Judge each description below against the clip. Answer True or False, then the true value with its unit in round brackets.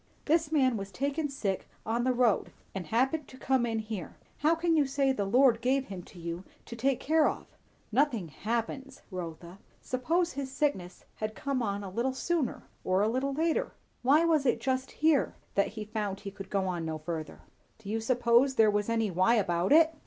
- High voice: True (235 Hz)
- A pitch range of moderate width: False (5.7 semitones)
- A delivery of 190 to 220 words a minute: True (195 wpm)